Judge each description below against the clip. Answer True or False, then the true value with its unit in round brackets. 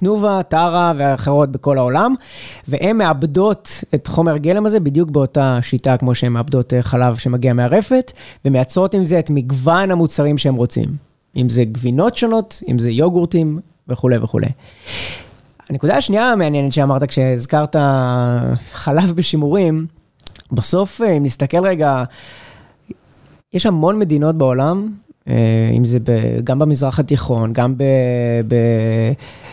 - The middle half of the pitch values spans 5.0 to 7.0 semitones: True (5.4 semitones)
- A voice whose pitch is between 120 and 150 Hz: True (140 Hz)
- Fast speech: False (125 wpm)